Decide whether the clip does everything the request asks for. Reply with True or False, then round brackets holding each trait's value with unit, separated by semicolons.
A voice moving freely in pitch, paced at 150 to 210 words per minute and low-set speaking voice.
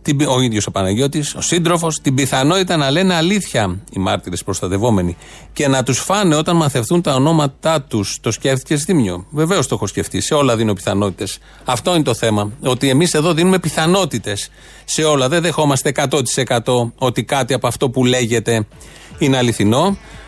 True (6.2 semitones; 165 wpm; 130 Hz)